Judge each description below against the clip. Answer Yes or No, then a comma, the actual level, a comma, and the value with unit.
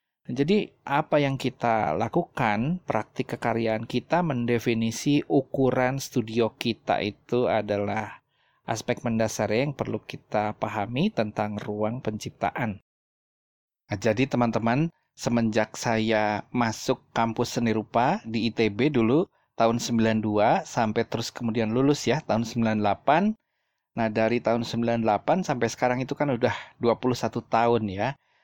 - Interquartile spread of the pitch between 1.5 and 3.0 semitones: Yes, average, 2.7 semitones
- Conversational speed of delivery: Yes, average, 120 wpm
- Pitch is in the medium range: No, low, 115 Hz